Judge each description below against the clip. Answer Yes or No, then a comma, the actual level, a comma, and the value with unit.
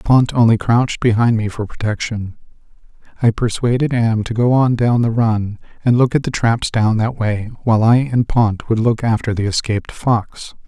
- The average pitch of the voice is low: Yes, low, 115 Hz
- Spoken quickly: No, average, 190 wpm